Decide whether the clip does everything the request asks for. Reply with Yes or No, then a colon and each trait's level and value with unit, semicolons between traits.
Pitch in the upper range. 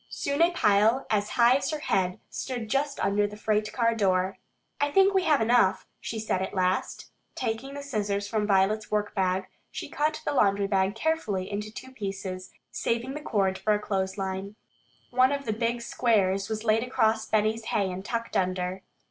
Yes: high, 215 Hz